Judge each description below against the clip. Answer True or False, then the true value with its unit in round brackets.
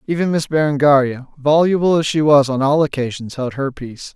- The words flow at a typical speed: True (190 wpm)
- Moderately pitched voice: True (145 Hz)